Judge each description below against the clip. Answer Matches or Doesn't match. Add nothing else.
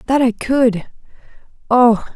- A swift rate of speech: Doesn't match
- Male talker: Doesn't match